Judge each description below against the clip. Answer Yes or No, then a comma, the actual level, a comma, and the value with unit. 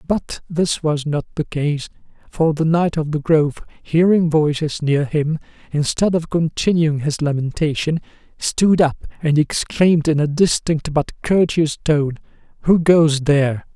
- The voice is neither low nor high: Yes, medium, 155 Hz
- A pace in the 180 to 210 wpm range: No, average, 150 wpm